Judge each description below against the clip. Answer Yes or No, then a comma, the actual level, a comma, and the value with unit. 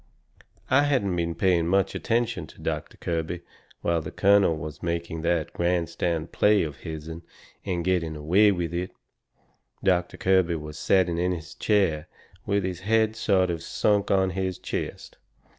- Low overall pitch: Yes, very low, 90 Hz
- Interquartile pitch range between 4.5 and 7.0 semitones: No, average, 2.8 semitones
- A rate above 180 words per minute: No, average, 155 wpm